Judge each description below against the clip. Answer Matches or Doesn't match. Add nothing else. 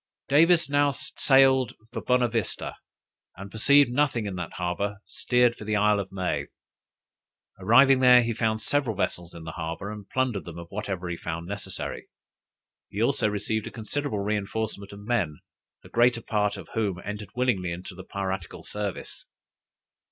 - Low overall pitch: Matches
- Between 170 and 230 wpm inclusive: Doesn't match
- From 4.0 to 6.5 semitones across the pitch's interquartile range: Matches